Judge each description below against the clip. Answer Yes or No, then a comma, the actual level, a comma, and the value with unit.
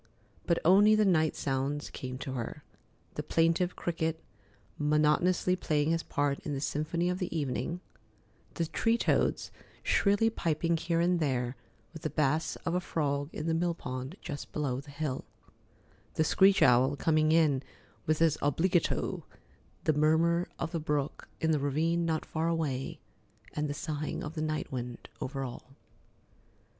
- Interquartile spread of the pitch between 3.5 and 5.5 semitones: No, average, 2.8 semitones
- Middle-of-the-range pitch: Yes, medium, 155 Hz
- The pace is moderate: Yes, average, 155 wpm